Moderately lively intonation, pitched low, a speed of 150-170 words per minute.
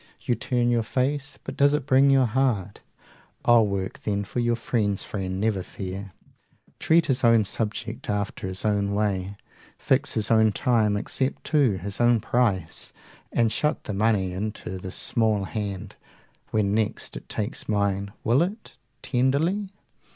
Yes: average, 3.6 semitones; low, 110 Hz; average, 160 wpm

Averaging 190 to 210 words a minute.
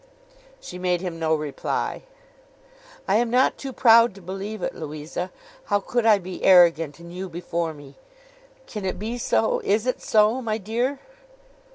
No: average, 165 wpm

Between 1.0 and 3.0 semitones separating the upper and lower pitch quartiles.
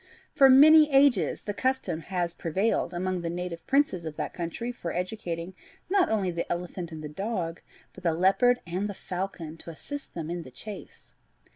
No: average, 5.1 semitones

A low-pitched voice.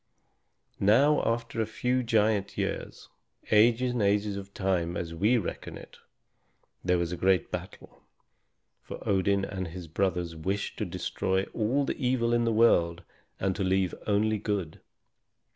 Yes: low, 100 Hz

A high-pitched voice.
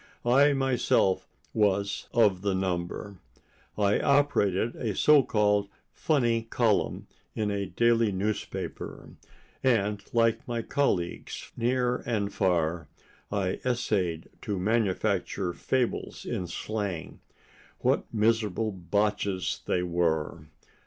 No: low, 105 Hz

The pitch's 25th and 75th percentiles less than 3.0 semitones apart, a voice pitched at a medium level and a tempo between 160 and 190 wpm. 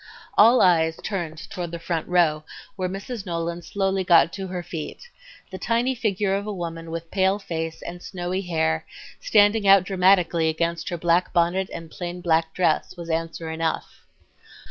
Yes: narrow, 2.6 semitones; medium, 175 Hz; average, 165 wpm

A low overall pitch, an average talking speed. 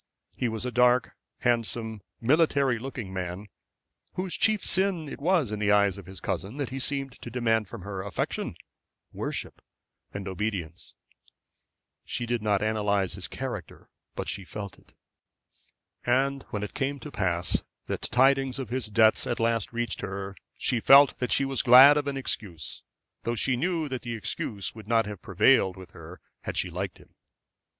Yes: low, 115 Hz; average, 175 wpm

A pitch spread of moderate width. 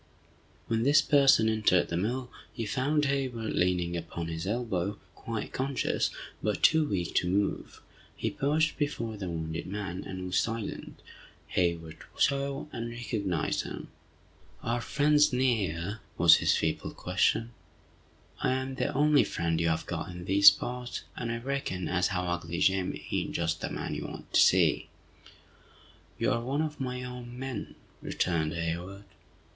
No: wide, 6.5 semitones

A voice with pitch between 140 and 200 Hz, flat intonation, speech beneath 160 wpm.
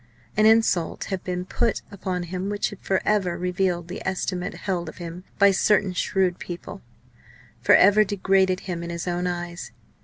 No: medium, 185 Hz; narrow, 1.9 semitones; average, 175 wpm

